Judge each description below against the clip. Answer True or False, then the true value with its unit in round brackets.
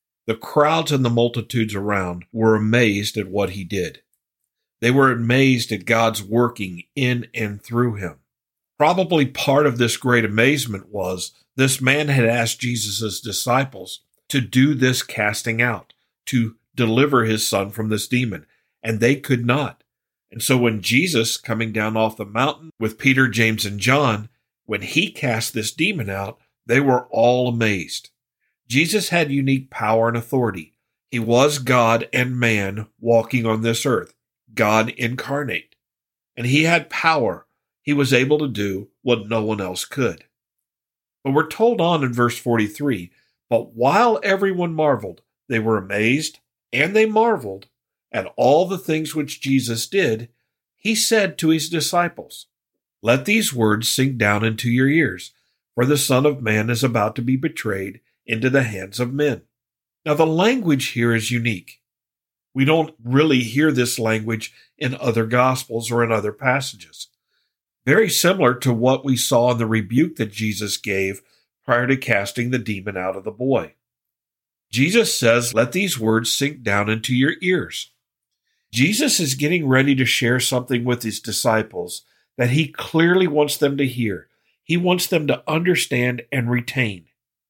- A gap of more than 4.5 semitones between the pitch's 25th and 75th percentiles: False (4.0 semitones)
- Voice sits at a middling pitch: False (120 Hz)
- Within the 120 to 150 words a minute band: False (160 wpm)